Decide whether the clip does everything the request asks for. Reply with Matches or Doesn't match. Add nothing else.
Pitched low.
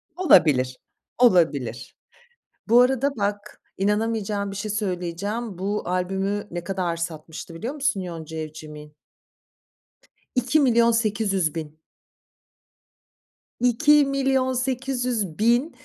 Doesn't match